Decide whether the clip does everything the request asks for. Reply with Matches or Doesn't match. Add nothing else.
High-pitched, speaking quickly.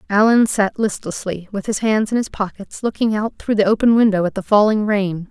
Matches